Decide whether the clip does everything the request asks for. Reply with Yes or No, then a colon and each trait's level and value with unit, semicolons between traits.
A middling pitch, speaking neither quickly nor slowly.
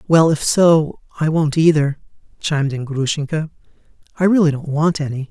Yes: medium, 155 Hz; average, 160 wpm